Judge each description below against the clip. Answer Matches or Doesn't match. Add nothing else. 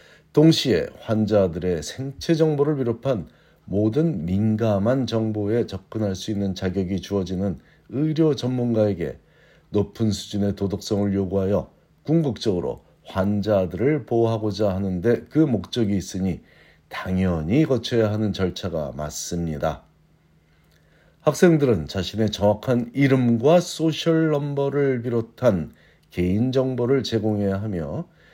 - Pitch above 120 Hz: Doesn't match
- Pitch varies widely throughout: Matches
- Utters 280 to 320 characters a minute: Doesn't match